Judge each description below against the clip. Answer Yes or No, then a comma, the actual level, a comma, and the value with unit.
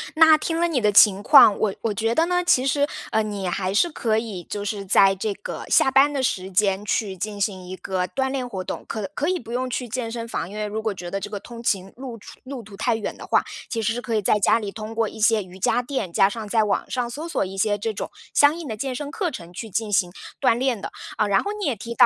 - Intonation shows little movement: No, average, 4.2 semitones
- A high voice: Yes, high, 220 Hz